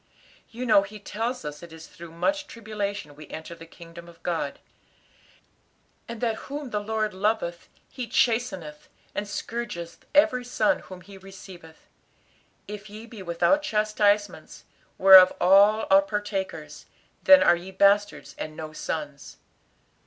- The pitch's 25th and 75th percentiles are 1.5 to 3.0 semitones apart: No, average, 4.4 semitones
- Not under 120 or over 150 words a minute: Yes, average, 140 wpm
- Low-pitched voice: No, high, 200 Hz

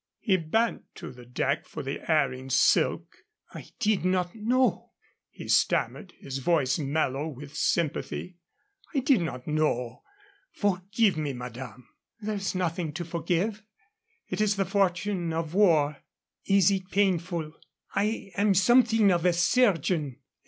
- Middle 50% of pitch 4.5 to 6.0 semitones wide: Yes, average, 5.1 semitones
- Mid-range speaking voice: Yes, medium, 175 Hz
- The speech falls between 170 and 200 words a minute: No, average, 140 wpm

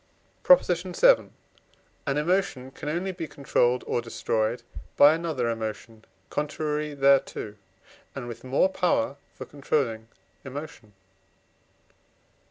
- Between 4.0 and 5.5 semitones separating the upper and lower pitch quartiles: Yes, average, 4.7 semitones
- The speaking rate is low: Yes, slow, 105 wpm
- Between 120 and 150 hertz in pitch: Yes, medium, 140 Hz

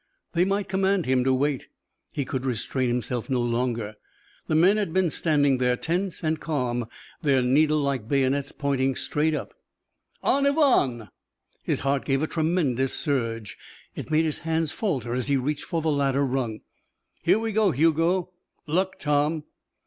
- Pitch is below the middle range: No, medium, 145 Hz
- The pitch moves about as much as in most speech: Yes, average, 4.3 semitones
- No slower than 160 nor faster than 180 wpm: Yes, average, 165 wpm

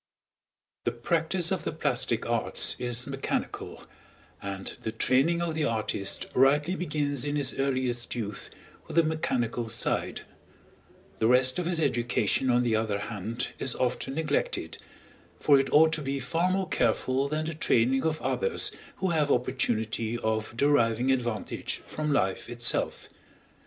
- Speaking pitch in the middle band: No, low, 130 Hz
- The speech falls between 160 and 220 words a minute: No, average, 145 wpm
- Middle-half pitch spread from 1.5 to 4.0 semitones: No, average, 4.6 semitones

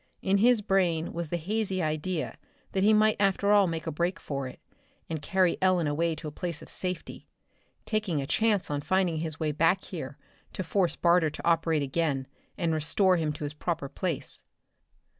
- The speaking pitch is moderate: Yes, medium, 170 Hz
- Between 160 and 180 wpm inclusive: No, average, 190 wpm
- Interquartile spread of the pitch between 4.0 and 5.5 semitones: No, average, 3.5 semitones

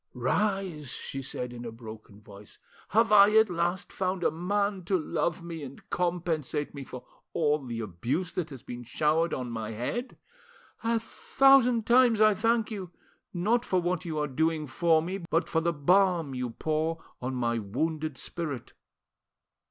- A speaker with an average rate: Yes, average, 165 wpm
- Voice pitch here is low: No, medium, 165 Hz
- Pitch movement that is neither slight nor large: No, wide, 6.6 semitones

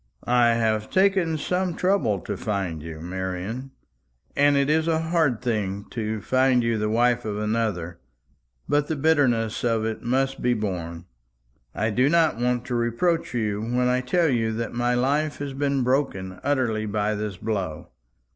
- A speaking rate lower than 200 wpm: Yes, average, 165 wpm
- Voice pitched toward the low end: Yes, low, 120 Hz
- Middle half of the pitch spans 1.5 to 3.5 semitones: No, average, 4.6 semitones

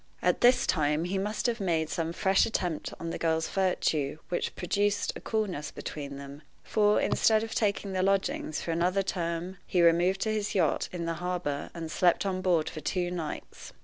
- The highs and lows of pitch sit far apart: No, average, 3.2 semitones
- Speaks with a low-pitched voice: No, medium, 180 Hz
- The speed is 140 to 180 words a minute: No, average, 190 wpm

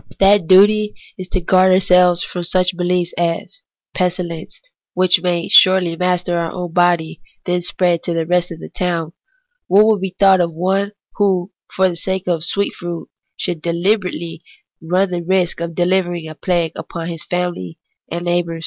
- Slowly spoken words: No, average, 185 wpm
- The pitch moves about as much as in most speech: No, narrow, 1.6 semitones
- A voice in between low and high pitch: Yes, medium, 180 Hz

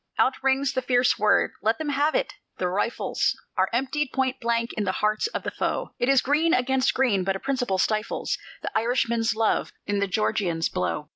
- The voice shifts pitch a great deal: No, average, 4.0 semitones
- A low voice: No, high, 240 Hz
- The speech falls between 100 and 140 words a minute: No, average, 200 wpm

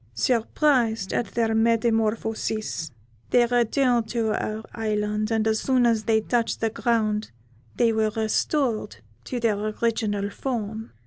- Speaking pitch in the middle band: No, high, 225 Hz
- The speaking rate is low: Yes, slow, 130 wpm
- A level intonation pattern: Yes, narrow, 1.6 semitones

